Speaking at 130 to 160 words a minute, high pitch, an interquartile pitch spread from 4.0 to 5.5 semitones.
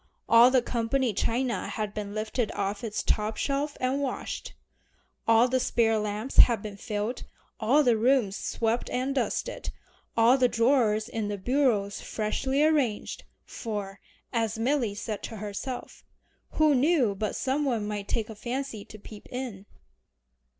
No: average, 150 wpm; high, 230 Hz; average, 3.5 semitones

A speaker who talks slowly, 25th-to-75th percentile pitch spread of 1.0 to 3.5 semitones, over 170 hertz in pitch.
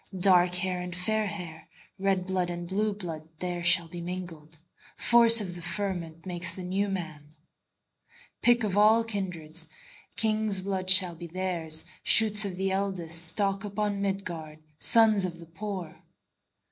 Yes: slow, 120 wpm; average, 2.9 semitones; medium, 185 Hz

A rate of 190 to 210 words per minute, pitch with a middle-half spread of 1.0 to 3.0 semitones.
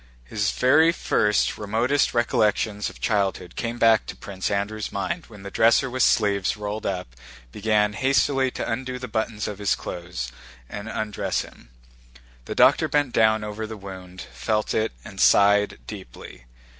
No: average, 155 wpm; narrow, 2.5 semitones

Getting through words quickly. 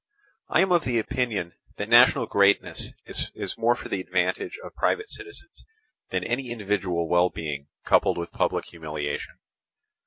No: average, 145 wpm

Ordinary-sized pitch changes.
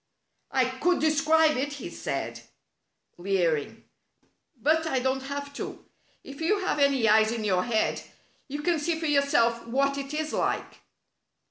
Yes: average, 4.7 semitones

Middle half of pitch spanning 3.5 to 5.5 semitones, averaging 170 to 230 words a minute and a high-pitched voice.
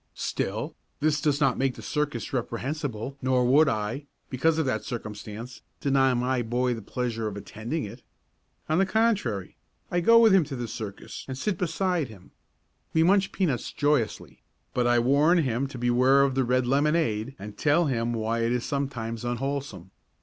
No: average, 4.3 semitones; average, 175 wpm; low, 130 Hz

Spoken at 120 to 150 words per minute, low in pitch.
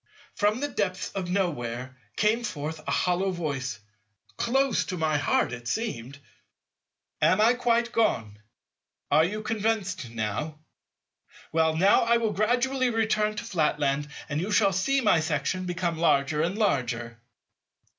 No: slow, 135 wpm; medium, 175 Hz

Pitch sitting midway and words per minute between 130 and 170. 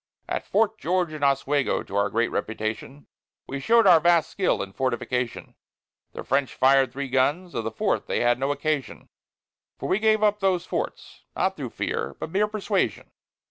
No: medium, 145 Hz; average, 180 wpm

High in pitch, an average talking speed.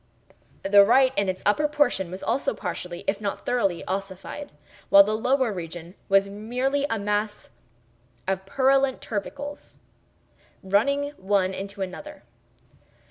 No: high, 205 Hz; slow, 130 wpm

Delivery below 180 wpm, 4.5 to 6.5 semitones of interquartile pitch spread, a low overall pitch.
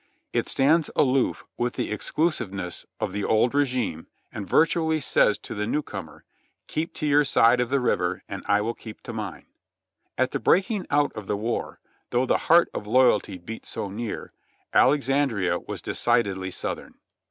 Yes: average, 170 wpm; wide, 5.6 semitones; low, 120 Hz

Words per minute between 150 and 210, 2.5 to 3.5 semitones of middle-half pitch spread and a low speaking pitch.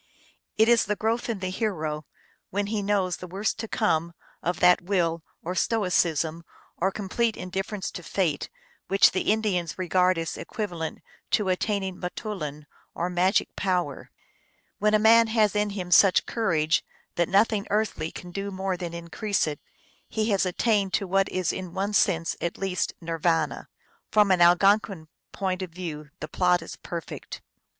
No: average, 170 wpm; average, 3.2 semitones; medium, 185 Hz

